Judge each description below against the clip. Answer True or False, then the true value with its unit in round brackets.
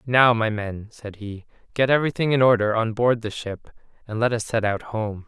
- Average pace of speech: False (215 wpm)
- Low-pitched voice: True (115 Hz)